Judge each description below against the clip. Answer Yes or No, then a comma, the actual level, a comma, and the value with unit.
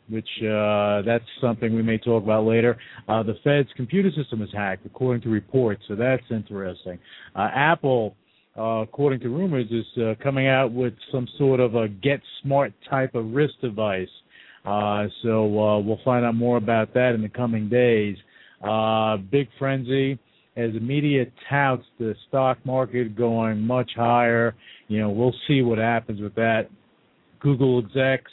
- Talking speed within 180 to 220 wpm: No, average, 165 wpm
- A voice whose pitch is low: Yes, low, 115 Hz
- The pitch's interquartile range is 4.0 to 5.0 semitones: No, average, 3.0 semitones